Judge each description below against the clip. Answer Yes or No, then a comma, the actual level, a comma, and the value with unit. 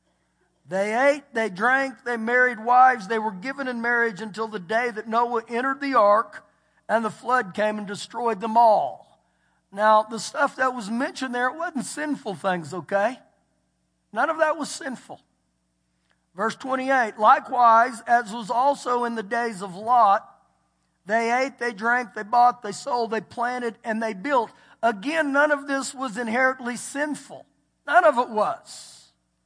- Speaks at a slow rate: No, average, 165 wpm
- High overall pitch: Yes, high, 235 Hz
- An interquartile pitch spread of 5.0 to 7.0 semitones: No, average, 3.4 semitones